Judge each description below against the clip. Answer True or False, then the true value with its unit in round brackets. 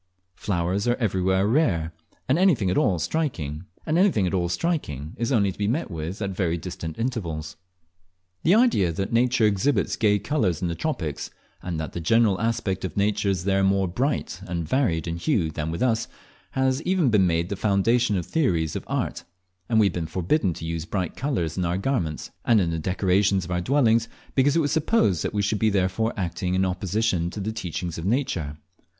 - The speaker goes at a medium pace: True (190 wpm)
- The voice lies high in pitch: False (95 Hz)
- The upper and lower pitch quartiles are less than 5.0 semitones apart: False (5.3 semitones)